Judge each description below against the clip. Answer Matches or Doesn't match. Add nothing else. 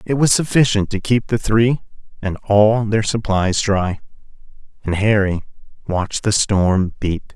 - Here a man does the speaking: Matches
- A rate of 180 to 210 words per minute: Doesn't match